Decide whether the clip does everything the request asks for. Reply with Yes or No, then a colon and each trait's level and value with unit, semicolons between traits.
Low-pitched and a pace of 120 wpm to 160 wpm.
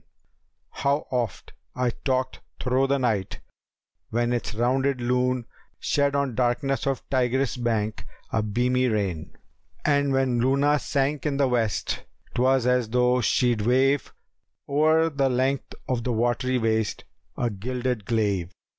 Yes: low, 125 Hz; average, 145 wpm